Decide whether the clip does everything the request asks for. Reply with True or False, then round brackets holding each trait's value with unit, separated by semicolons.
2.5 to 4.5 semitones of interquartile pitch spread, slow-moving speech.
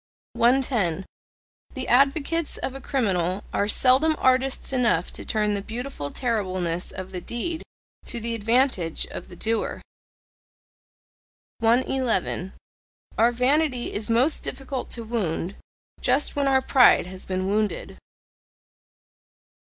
False (5.4 semitones; 120 wpm)